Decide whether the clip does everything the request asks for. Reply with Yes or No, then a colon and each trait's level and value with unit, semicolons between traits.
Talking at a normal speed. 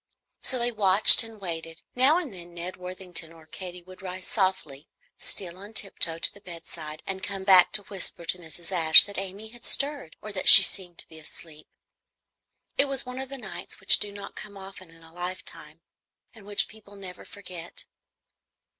Yes: average, 190 wpm